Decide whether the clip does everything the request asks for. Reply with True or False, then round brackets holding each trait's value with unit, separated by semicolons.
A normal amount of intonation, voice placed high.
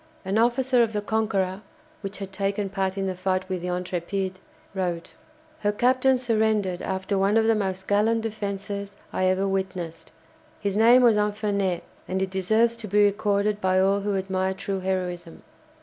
False (2.1 semitones; 195 Hz)